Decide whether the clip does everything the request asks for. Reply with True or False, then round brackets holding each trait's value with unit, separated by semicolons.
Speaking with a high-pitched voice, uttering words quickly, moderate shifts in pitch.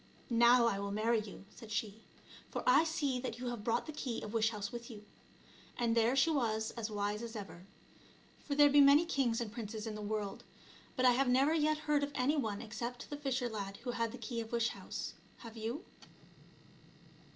True (235 Hz; 220 wpm; 3.4 semitones)